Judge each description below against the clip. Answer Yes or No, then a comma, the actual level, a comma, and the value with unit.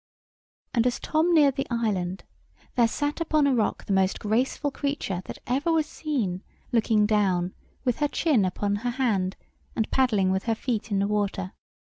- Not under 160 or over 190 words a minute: Yes, average, 175 wpm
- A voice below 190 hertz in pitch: No, high, 225 Hz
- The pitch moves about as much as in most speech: No, wide, 5.7 semitones